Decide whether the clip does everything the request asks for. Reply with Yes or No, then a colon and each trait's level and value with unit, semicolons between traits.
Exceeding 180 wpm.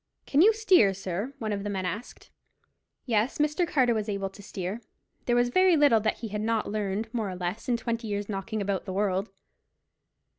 Yes: average, 200 wpm